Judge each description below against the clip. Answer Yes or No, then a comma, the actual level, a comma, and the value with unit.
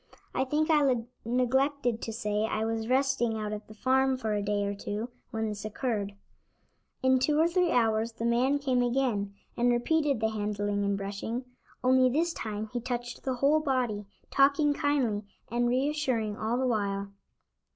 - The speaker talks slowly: No, average, 170 wpm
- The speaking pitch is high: Yes, high, 240 Hz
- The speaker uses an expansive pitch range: No, average, 3.8 semitones